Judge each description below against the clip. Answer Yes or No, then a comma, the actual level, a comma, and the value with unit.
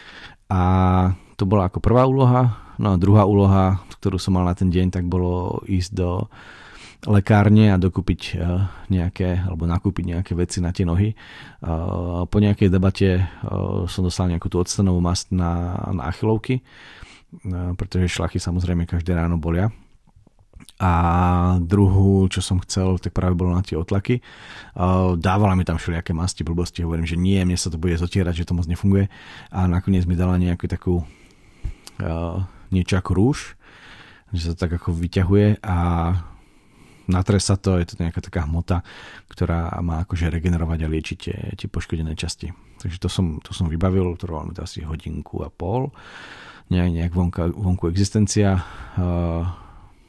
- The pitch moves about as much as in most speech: No, narrow, 2.0 semitones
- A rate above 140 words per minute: Yes, average, 155 wpm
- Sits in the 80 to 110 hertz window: Yes, very low, 90 Hz